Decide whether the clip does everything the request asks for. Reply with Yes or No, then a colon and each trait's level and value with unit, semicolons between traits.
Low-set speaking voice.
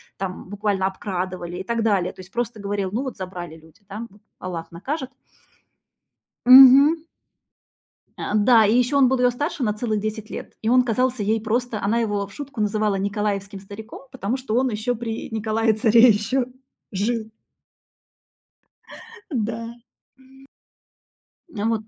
No: high, 220 Hz